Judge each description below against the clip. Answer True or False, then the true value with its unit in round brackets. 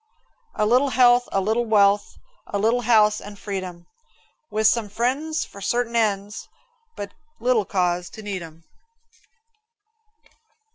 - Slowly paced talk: True (130 wpm)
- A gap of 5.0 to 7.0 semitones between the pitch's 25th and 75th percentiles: False (3.2 semitones)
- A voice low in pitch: False (210 Hz)